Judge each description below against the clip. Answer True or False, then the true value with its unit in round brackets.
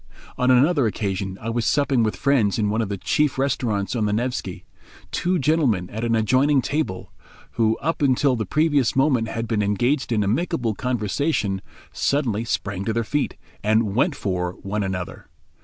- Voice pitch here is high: False (115 Hz)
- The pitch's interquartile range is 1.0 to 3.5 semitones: False (5.0 semitones)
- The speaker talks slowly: False (175 wpm)